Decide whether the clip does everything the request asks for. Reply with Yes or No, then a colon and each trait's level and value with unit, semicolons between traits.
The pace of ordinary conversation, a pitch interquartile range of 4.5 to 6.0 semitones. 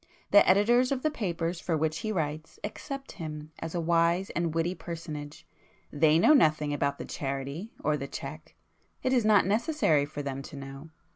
Yes: average, 175 wpm; average, 5.3 semitones